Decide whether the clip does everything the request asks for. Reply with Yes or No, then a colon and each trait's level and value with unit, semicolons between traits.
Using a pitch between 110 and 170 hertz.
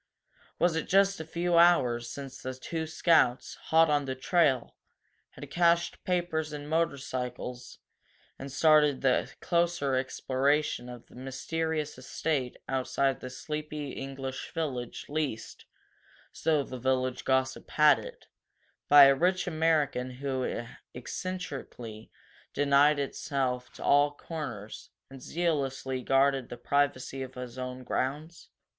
Yes: medium, 140 Hz